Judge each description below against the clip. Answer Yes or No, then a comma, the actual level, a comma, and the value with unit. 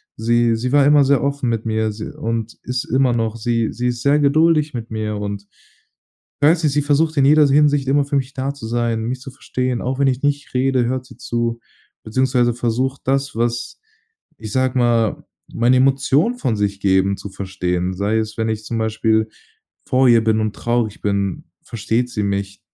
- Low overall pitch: Yes, low, 120 Hz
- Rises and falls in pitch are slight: No, average, 3.6 semitones